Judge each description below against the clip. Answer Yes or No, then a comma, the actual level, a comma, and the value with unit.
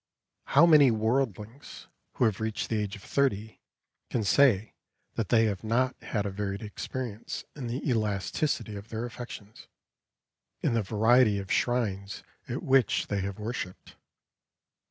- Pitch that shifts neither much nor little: Yes, average, 3.3 semitones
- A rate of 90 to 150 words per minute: Yes, average, 145 wpm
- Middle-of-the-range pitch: No, low, 110 Hz